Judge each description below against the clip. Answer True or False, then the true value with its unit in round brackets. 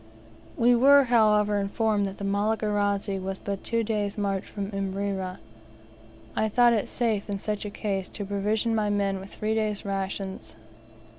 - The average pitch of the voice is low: False (205 Hz)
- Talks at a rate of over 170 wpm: False (160 wpm)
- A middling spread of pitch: False (1.7 semitones)